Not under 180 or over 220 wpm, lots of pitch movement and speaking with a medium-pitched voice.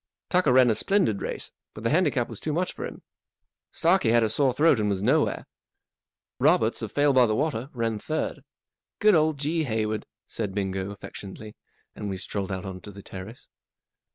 No: average, 190 wpm; wide, 6.5 semitones; low, 115 Hz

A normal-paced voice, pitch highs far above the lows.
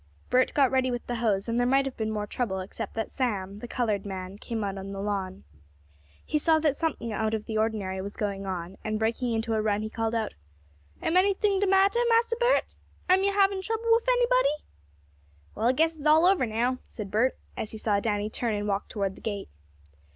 No: fast, 220 wpm; wide, 6.9 semitones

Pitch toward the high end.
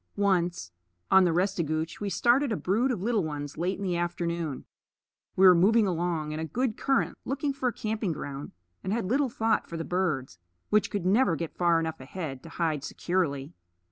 No: medium, 180 Hz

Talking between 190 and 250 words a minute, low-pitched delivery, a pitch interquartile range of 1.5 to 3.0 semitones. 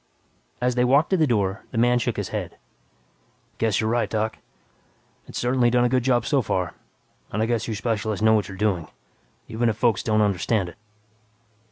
Yes: average, 195 wpm; low, 115 Hz; narrow, 2.4 semitones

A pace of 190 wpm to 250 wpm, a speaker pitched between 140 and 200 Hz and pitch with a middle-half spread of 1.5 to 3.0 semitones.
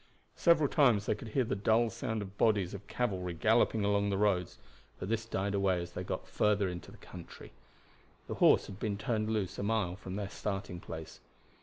No: average, 200 wpm; low, 100 Hz; narrow, 2.6 semitones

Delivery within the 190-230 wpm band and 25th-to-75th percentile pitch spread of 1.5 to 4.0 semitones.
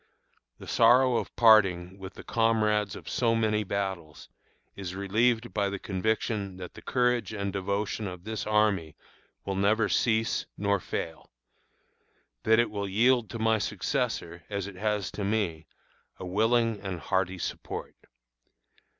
No: average, 145 wpm; average, 2.7 semitones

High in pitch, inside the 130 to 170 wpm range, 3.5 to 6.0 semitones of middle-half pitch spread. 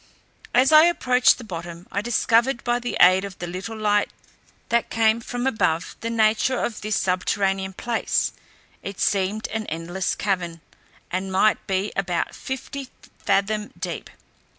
Yes: high, 210 Hz; average, 150 wpm; average, 3.9 semitones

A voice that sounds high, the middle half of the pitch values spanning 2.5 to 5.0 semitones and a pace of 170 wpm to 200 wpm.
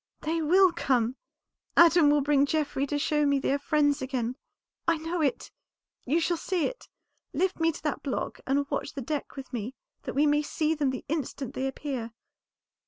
Yes: very high, 290 Hz; average, 3.0 semitones; average, 190 wpm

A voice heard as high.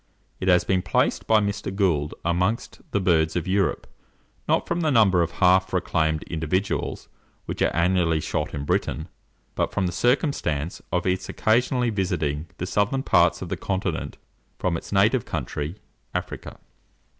No: very low, 90 Hz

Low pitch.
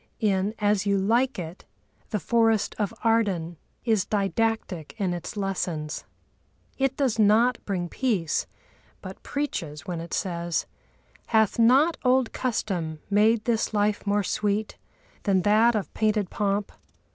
No: high, 210 Hz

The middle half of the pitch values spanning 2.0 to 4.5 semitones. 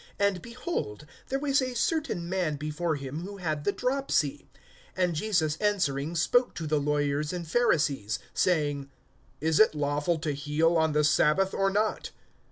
No: average, 5.3 semitones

